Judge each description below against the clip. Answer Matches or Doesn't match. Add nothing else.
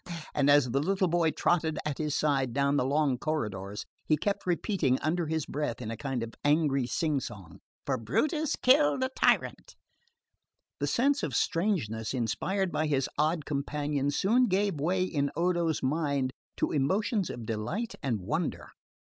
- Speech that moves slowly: Doesn't match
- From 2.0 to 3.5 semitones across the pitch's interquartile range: Doesn't match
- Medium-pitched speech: Matches